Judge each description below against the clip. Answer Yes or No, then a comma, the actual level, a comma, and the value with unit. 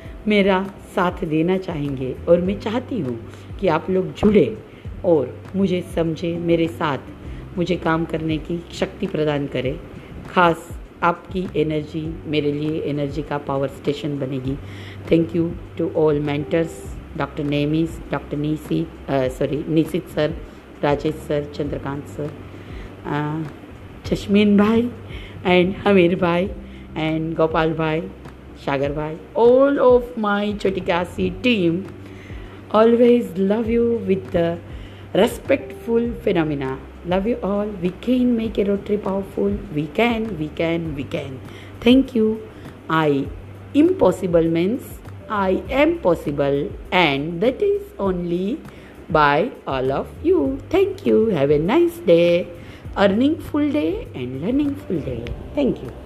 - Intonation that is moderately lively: No, wide, 5.8 semitones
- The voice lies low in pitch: No, medium, 170 Hz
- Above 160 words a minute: No, average, 125 wpm